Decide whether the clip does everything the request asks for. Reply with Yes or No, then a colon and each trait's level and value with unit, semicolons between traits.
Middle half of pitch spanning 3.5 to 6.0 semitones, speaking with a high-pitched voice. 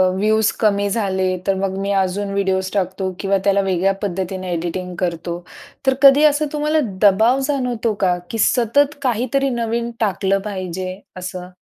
Yes: average, 3.8 semitones; high, 200 Hz